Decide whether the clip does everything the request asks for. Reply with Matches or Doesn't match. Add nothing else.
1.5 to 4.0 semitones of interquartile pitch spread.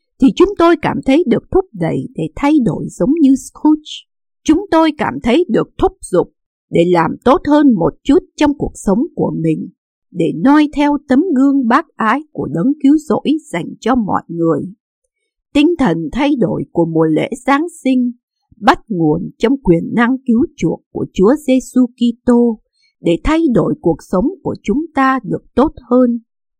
Doesn't match